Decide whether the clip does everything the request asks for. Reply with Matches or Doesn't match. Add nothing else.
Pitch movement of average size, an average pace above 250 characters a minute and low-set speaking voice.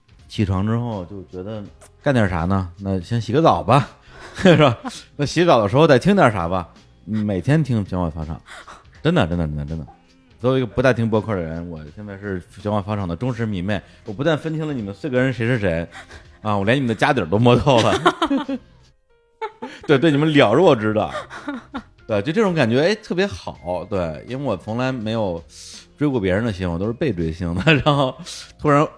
Doesn't match